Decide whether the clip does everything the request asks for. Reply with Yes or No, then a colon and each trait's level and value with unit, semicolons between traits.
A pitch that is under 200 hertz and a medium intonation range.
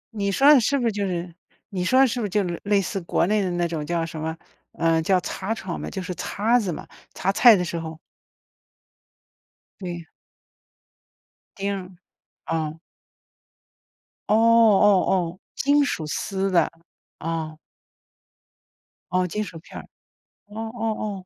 Yes: high, 190 Hz; average, 3.9 semitones